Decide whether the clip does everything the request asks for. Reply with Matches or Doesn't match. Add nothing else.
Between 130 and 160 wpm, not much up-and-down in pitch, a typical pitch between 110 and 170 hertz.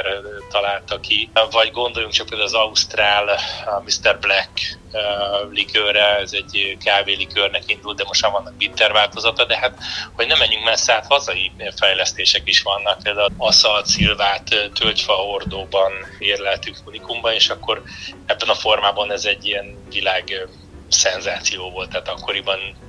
Doesn't match